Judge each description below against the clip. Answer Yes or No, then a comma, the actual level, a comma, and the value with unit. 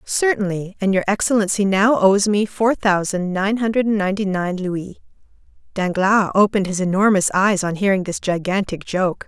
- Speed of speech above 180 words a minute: No, average, 155 wpm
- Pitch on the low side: No, high, 195 Hz